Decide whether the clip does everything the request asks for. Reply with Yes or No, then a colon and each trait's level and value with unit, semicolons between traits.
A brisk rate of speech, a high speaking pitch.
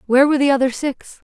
Yes: fast, 230 wpm; very high, 270 Hz